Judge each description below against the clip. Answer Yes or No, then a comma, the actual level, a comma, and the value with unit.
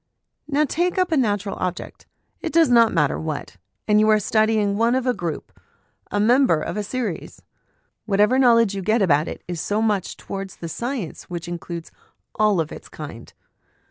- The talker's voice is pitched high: Yes, high, 210 Hz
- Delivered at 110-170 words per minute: No, average, 180 wpm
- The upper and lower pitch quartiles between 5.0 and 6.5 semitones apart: Yes, wide, 5.4 semitones